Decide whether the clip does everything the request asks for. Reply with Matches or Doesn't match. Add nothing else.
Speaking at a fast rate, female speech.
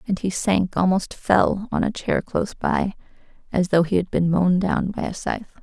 Matches